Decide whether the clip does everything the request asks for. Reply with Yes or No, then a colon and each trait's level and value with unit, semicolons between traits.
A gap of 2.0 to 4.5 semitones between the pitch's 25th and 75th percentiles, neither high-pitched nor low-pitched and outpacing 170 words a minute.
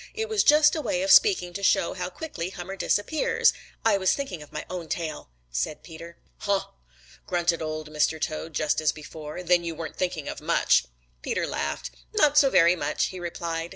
Yes: average, 4.0 semitones; medium, 175 Hz; average, 190 wpm